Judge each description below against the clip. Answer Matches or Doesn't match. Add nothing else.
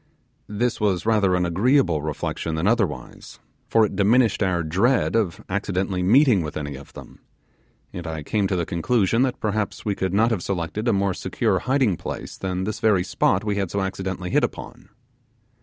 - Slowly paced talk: Doesn't match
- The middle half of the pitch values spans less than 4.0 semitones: Matches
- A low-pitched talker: Matches